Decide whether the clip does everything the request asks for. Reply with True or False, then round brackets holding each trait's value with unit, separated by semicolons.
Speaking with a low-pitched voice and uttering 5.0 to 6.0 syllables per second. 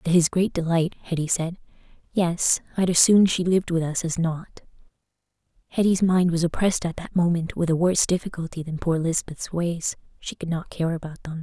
False (170 Hz; 5.4 syllables/s)